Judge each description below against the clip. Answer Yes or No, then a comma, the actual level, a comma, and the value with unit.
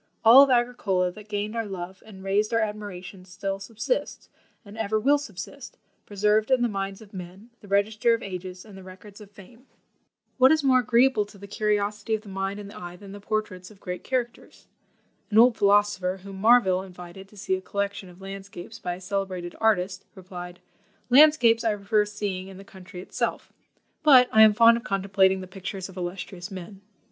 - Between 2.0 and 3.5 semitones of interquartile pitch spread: Yes, narrow, 2.6 semitones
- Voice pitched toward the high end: Yes, high, 200 Hz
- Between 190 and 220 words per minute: Yes, average, 195 wpm